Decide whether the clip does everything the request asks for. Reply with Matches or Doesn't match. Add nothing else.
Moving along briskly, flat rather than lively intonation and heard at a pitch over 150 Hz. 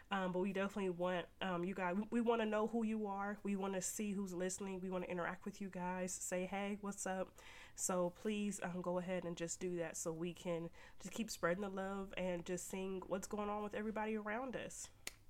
Matches